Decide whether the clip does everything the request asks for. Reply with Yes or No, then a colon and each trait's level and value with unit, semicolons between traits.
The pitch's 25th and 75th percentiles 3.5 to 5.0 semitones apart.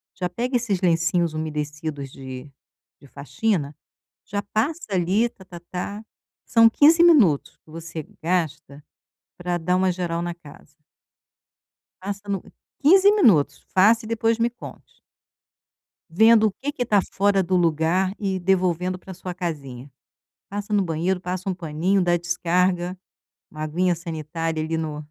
Yes: average, 3.9 semitones